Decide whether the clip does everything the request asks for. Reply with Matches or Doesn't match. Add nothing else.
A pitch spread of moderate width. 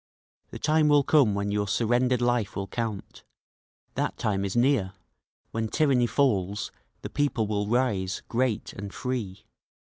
Matches